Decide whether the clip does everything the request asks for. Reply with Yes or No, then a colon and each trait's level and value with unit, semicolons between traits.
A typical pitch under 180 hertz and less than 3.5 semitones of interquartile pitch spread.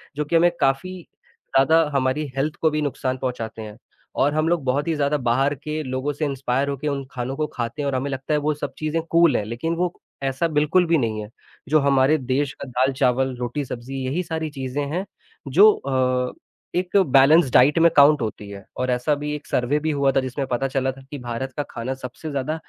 Yes: medium, 140 Hz; average, 2.9 semitones